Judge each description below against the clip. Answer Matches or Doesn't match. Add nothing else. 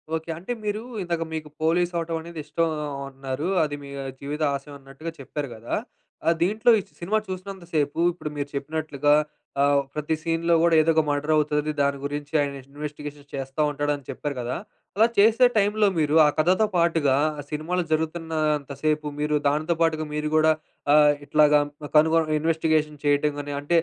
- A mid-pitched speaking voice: Matches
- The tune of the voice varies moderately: Doesn't match